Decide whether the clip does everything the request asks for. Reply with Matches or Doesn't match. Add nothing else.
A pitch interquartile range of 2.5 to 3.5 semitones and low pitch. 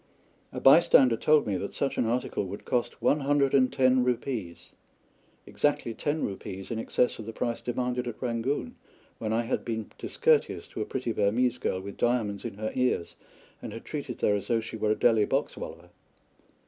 Matches